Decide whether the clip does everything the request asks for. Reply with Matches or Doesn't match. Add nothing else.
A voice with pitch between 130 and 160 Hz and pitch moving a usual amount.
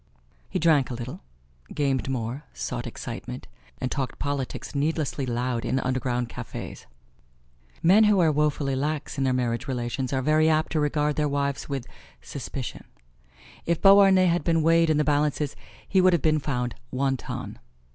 Matches